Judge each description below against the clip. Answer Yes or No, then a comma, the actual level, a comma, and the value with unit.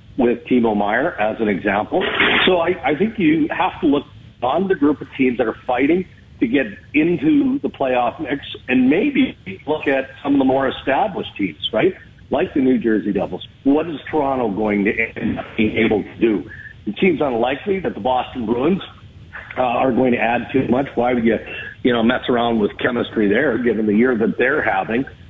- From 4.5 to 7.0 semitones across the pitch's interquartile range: Yes, average, 5.2 semitones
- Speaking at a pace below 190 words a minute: No, average, 200 wpm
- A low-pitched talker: Yes, low, 130 Hz